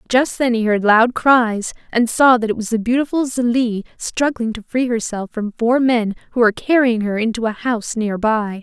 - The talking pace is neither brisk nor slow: No, fast, 210 wpm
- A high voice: Yes, high, 230 Hz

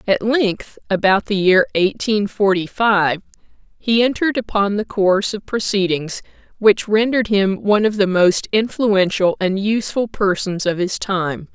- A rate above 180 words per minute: No, average, 150 wpm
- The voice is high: Yes, high, 200 Hz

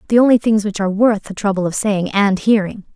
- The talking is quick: Yes, fast, 245 wpm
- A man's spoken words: No, female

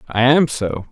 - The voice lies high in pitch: No, low, 125 Hz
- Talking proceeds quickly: No, average, 195 wpm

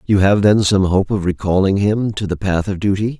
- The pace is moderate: No, fast, 245 wpm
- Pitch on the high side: No, low, 100 Hz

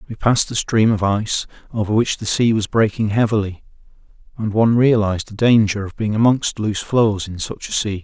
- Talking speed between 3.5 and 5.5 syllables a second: No, 5.7 syllables/s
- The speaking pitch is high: No, low, 110 Hz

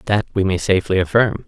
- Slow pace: No, fast, 205 wpm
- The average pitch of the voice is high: No, low, 100 Hz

